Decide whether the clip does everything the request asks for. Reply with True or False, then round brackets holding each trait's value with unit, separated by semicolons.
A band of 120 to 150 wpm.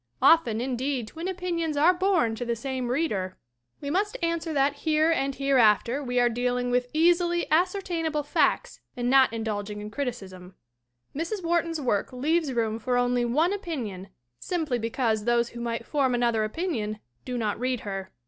False (165 wpm)